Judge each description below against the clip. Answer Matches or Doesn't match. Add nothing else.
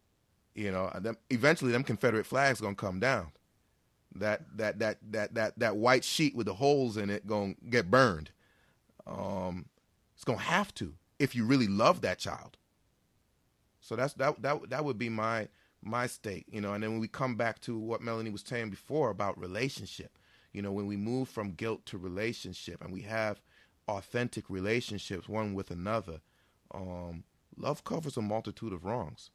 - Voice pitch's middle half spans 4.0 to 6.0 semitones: Doesn't match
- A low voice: Matches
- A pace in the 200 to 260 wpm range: Doesn't match